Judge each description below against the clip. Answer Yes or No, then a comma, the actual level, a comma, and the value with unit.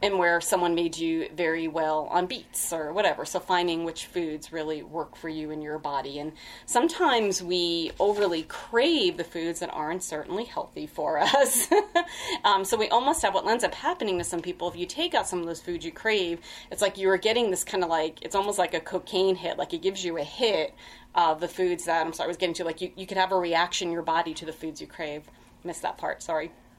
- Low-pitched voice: No, medium, 175 Hz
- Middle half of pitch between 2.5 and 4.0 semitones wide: Yes, average, 3.0 semitones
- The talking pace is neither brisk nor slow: No, fast, 240 wpm